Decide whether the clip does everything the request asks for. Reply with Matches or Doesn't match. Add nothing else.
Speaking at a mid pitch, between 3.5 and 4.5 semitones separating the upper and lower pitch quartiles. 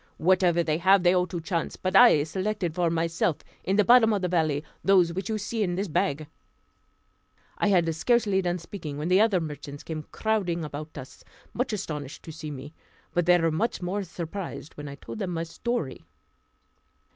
Matches